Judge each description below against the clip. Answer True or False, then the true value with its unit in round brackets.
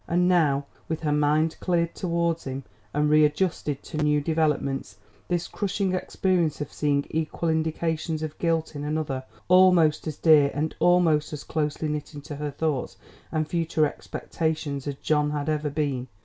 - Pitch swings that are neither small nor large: False (2.1 semitones)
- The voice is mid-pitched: True (155 Hz)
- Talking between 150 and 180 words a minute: True (160 wpm)